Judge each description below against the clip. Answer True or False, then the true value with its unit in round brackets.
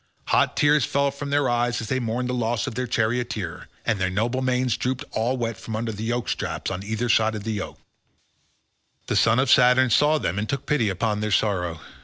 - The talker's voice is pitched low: True (120 Hz)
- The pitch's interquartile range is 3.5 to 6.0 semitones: False (2.9 semitones)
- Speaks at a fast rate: True (215 wpm)